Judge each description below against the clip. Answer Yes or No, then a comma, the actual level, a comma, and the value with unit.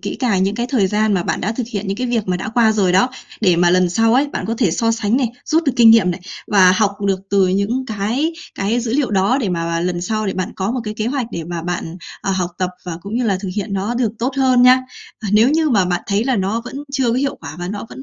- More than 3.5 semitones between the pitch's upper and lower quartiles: Yes, average, 4.4 semitones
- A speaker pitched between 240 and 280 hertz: No, high, 210 Hz